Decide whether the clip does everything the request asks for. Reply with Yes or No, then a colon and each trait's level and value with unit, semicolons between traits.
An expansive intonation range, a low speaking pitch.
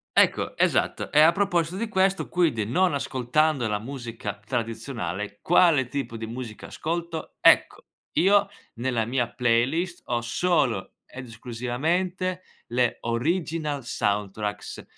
Yes: wide, 6.7 semitones; low, 130 Hz